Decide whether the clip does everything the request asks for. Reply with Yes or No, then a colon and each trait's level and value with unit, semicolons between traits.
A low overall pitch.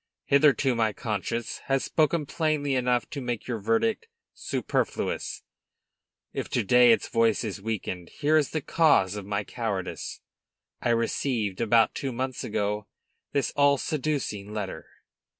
Yes: low, 120 Hz